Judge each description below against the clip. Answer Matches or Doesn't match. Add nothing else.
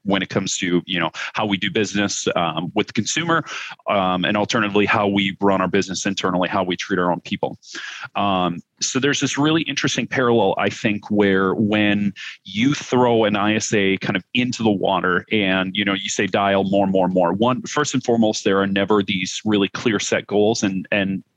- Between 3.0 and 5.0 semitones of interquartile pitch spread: Doesn't match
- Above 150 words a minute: Matches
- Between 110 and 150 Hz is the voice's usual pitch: Doesn't match